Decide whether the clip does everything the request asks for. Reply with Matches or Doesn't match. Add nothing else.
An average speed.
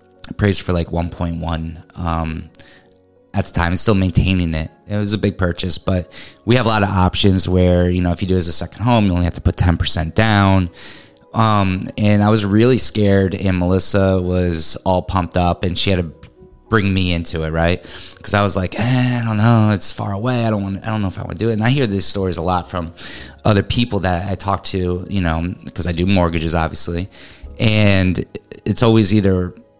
Doesn't match